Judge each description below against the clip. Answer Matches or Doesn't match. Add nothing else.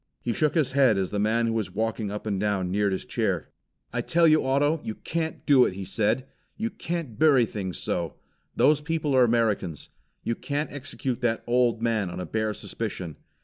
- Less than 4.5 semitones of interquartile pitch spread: Doesn't match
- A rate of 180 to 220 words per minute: Matches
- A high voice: Doesn't match